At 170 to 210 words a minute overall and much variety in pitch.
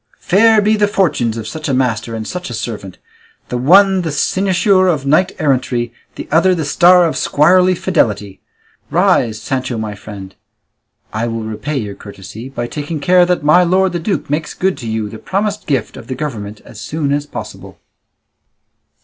Yes: average, 180 wpm; wide, 8.0 semitones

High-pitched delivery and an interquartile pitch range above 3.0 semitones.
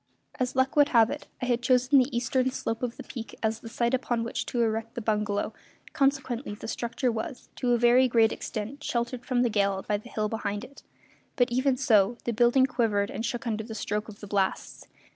No: high, 235 Hz; narrow, 2.5 semitones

